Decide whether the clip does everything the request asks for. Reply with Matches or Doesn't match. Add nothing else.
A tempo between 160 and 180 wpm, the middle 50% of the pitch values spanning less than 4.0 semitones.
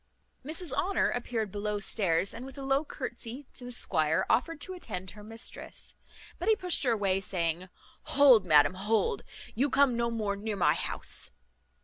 Doesn't match